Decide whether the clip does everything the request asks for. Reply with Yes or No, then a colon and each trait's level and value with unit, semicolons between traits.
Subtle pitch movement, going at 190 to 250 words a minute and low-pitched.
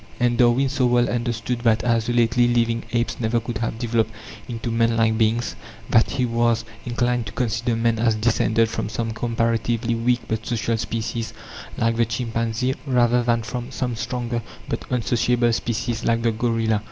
No: narrow, 1.1 semitones; average, 165 wpm; low, 115 Hz